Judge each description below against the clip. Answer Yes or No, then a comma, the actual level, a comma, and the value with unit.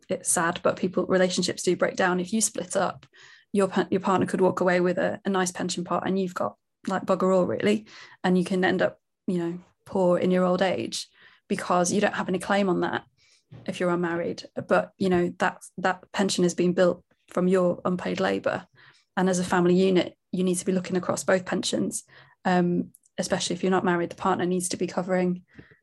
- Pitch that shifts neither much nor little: No, narrow, 1.0 semitones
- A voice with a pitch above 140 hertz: Yes, medium, 185 Hz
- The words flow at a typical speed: No, fast, 215 wpm